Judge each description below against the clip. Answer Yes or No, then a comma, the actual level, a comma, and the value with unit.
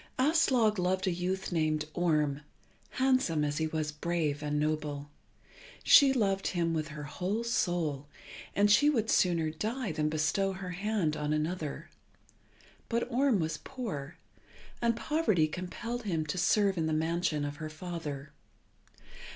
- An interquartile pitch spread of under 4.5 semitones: No, wide, 5.5 semitones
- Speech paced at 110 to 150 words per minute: Yes, average, 145 wpm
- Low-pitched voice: No, medium, 170 Hz